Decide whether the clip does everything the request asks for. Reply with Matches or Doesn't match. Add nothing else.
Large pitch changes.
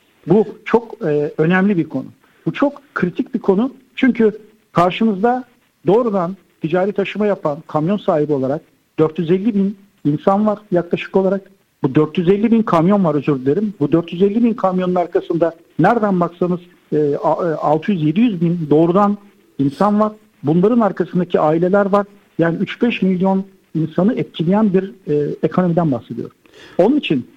Doesn't match